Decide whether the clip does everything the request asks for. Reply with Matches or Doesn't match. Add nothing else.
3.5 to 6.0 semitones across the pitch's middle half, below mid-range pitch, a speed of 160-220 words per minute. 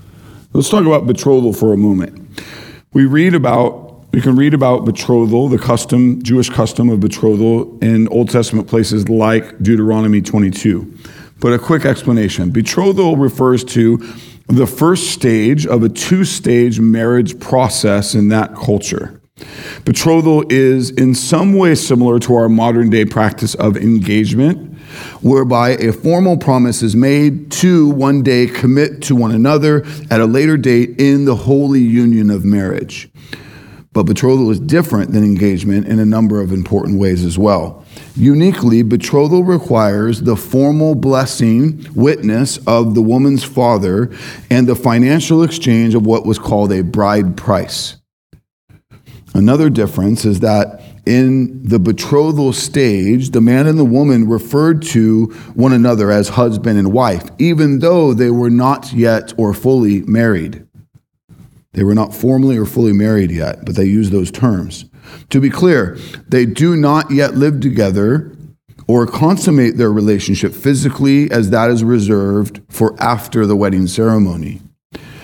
Doesn't match